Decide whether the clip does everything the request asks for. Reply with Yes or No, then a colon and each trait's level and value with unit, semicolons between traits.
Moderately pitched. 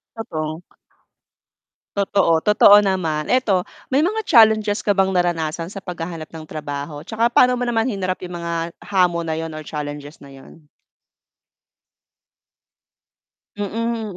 Yes: medium, 180 Hz